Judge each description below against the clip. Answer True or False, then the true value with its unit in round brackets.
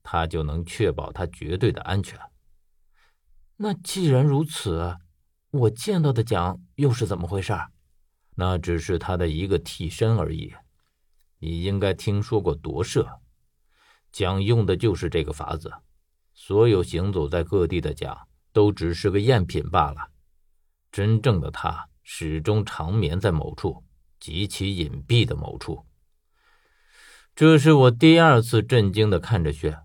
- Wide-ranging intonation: True (6.1 semitones)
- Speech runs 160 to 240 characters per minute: True (205 characters per minute)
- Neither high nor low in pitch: False (95 Hz)